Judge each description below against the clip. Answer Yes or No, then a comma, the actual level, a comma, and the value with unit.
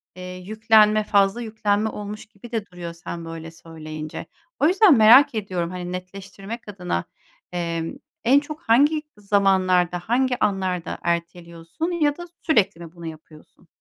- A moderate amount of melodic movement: Yes, average, 4.5 semitones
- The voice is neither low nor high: No, high, 195 Hz